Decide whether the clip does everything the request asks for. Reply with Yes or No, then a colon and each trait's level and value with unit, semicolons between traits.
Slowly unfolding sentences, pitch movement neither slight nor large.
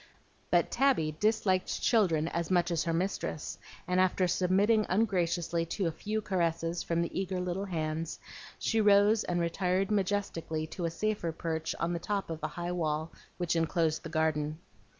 No: average, 170 wpm; average, 3.0 semitones